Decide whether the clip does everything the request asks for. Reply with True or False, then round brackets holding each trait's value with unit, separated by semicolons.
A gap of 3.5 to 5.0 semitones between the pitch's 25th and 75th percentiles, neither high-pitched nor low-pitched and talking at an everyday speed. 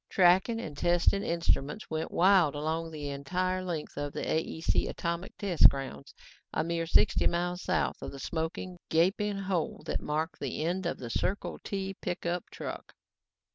False (2.9 semitones; 170 Hz; 160 wpm)